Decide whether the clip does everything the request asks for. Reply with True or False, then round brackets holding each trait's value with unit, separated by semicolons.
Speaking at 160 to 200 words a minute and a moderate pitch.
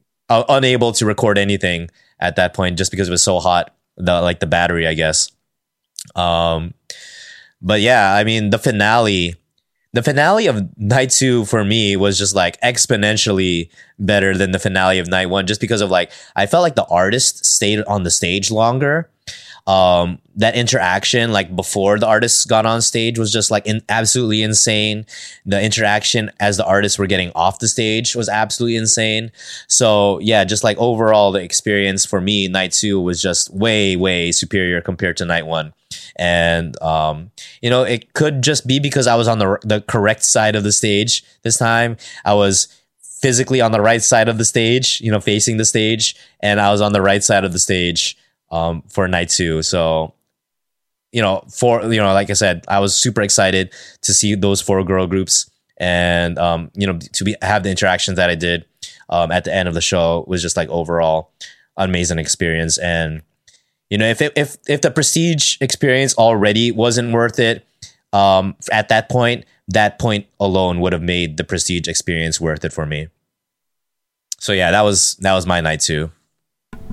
False (190 wpm; 100 Hz)